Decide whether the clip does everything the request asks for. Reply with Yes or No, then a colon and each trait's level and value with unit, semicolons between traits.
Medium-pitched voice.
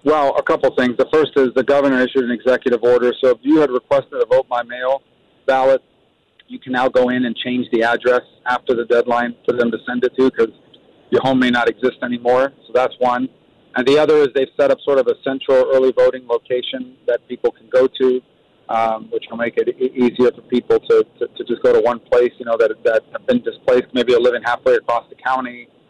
No: low, 130 Hz